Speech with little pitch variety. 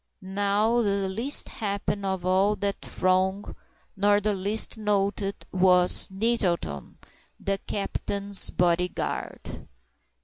Yes: narrow, 1.6 semitones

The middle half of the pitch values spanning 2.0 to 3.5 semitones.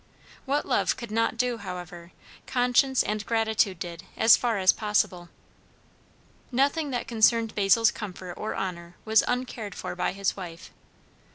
No: average, 4.3 semitones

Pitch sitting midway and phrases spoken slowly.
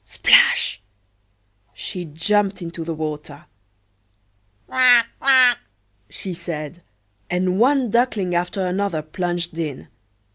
Yes: medium, 180 Hz; slow, 100 wpm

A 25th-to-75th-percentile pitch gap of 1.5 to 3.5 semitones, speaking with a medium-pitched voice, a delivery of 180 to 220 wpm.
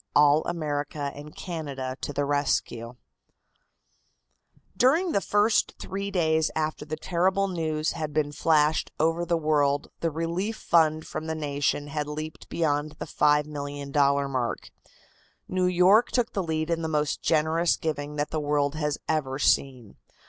No: narrow, 2.4 semitones; medium, 155 Hz; average, 150 wpm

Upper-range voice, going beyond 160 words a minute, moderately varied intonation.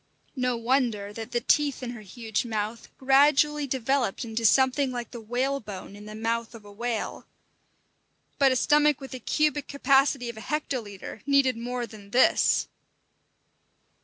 No: high, 245 Hz; average, 155 wpm; average, 3.5 semitones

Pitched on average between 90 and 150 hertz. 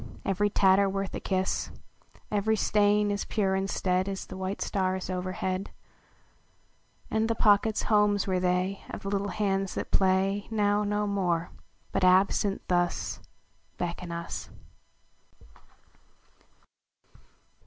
No: high, 195 Hz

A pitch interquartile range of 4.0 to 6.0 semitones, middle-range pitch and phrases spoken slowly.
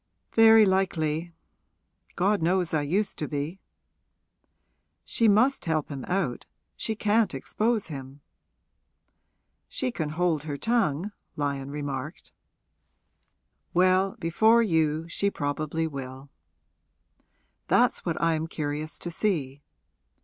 Yes: average, 5.1 semitones; medium, 165 Hz; slow, 110 wpm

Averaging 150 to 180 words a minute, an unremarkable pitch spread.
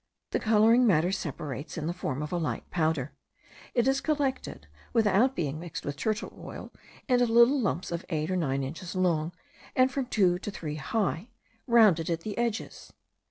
No: average, 170 wpm; wide, 6.6 semitones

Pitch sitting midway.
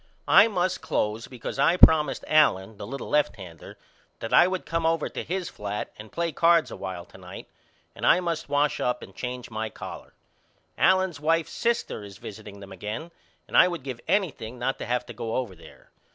No: low, 130 Hz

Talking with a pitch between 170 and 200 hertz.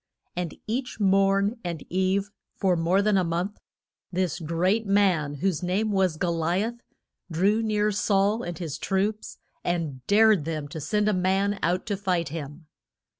Yes: high, 190 Hz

